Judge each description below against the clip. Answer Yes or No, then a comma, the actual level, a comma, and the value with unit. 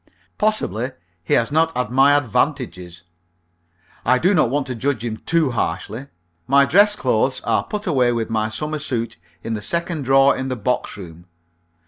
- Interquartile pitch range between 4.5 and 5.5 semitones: Yes, average, 5.1 semitones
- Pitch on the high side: No, low, 130 Hz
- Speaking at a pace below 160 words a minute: No, average, 170 wpm